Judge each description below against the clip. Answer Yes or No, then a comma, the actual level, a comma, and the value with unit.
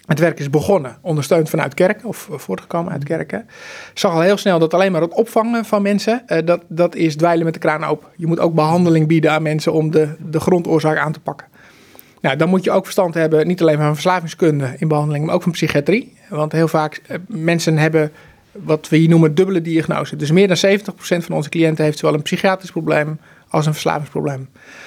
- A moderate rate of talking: No, fast, 210 wpm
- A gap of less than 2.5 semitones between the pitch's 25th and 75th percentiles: No, average, 2.9 semitones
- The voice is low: No, medium, 165 Hz